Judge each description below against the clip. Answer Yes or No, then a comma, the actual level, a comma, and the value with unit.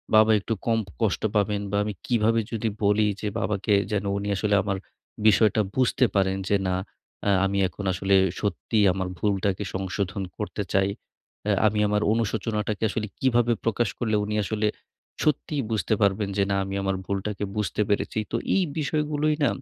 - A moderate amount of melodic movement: No, narrow, 2.2 semitones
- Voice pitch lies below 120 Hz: Yes, low, 105 Hz